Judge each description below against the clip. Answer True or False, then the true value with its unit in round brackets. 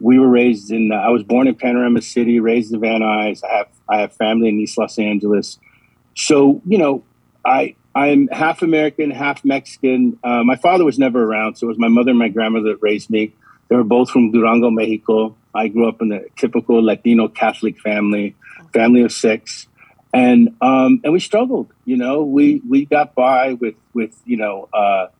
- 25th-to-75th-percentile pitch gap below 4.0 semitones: True (3.0 semitones)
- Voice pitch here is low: True (120 Hz)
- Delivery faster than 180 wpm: True (200 wpm)